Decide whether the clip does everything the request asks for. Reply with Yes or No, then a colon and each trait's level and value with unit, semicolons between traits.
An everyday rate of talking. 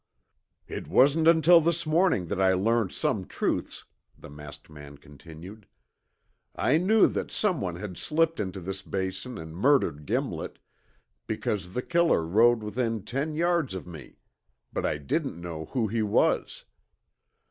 Yes: average, 145 wpm